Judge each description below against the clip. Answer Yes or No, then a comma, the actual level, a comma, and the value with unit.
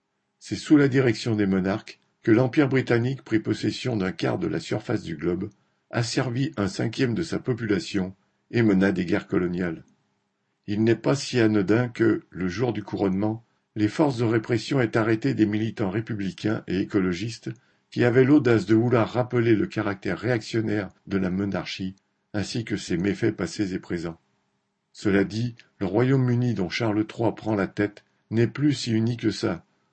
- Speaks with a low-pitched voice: Yes, low, 110 Hz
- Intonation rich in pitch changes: No, average, 3.2 semitones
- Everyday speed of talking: Yes, average, 170 wpm